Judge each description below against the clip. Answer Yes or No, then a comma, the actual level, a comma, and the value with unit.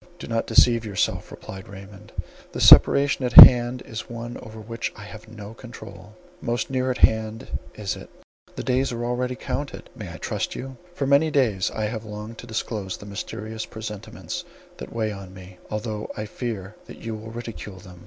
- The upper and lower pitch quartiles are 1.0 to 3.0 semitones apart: Yes, narrow, 2.5 semitones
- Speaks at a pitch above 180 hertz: No, low, 110 Hz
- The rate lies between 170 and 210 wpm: Yes, average, 185 wpm